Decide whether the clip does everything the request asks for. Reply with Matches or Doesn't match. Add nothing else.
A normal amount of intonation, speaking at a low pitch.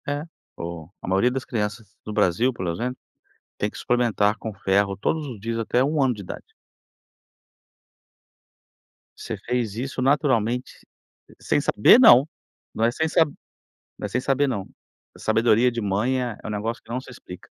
Matches